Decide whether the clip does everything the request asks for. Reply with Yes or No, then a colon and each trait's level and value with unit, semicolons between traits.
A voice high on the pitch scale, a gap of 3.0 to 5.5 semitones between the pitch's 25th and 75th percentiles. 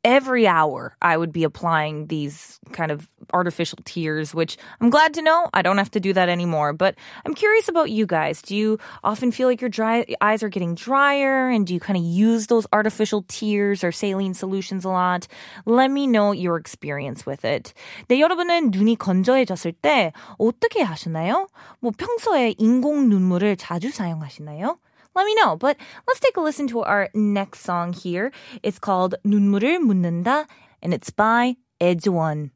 No: high, 205 Hz; wide, 6.4 semitones